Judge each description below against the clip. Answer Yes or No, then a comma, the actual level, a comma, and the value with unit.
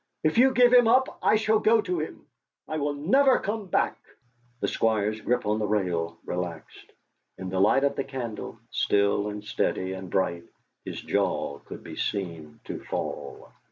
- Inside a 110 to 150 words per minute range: No, average, 175 wpm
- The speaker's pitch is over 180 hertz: No, low, 110 Hz